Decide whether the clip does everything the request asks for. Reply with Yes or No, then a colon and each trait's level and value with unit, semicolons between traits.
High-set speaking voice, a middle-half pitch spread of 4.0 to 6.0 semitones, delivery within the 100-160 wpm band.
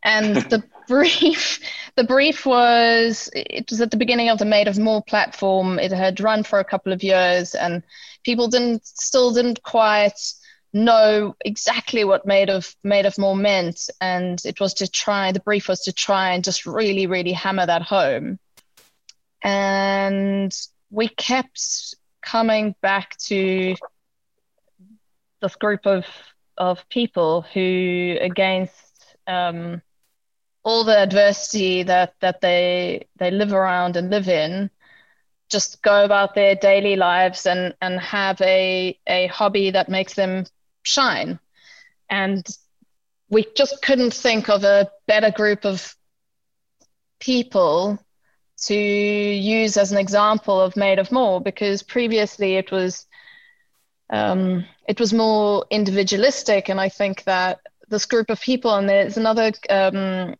No: high, 200 Hz; average, 2.8 semitones; average, 140 wpm